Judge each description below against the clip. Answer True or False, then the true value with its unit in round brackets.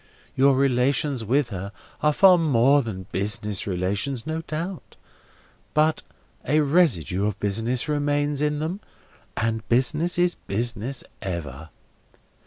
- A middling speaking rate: False (120 wpm)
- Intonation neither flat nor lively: False (6.2 semitones)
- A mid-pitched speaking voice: False (130 Hz)